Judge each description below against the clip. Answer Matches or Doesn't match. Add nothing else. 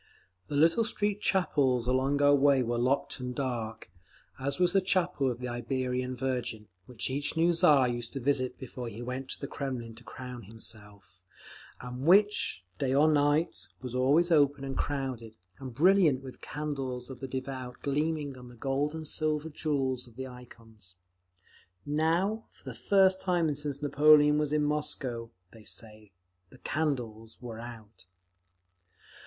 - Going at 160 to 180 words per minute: Matches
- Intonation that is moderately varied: Matches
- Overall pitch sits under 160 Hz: Matches